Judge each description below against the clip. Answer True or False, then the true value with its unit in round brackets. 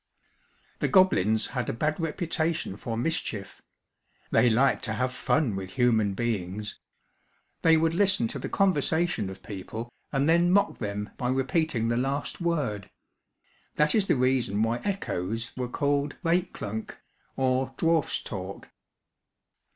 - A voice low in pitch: True (130 Hz)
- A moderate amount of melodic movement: False (6.7 semitones)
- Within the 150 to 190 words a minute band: False (140 wpm)